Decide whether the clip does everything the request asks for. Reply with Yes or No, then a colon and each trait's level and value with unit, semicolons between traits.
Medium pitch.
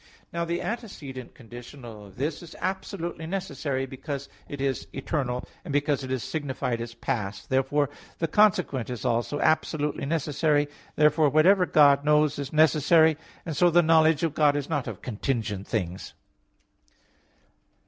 Yes: medium, 145 Hz